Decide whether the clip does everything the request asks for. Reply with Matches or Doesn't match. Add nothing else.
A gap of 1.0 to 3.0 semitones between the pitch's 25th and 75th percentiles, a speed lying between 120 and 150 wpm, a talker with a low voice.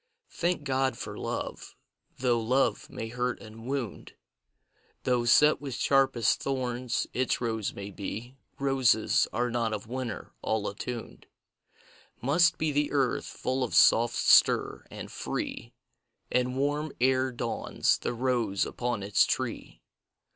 Matches